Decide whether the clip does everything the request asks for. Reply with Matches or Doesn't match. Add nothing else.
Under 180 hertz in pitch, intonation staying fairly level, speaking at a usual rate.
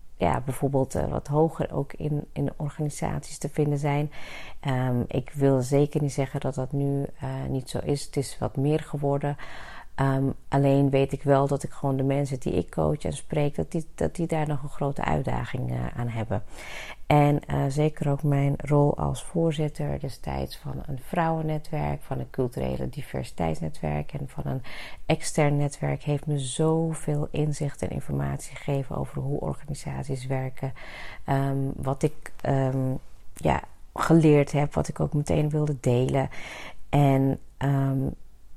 Matches